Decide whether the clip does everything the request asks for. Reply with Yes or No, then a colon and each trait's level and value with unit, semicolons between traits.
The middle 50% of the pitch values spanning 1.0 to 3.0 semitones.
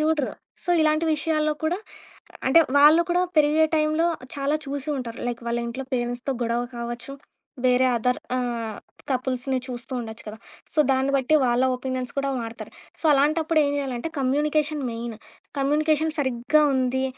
No: average, 3.8 semitones